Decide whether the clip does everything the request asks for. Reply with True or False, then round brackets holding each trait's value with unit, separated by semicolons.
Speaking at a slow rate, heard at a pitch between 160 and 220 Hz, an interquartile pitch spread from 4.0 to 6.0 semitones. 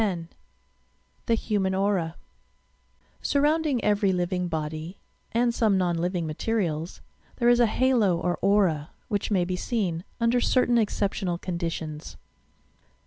True (130 wpm; 190 Hz; 4.9 semitones)